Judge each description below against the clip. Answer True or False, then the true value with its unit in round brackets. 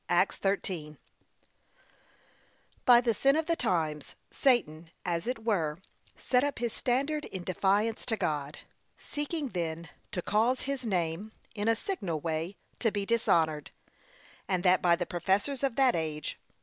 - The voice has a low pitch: False (200 Hz)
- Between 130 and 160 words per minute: True (150 wpm)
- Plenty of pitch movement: True (6.7 semitones)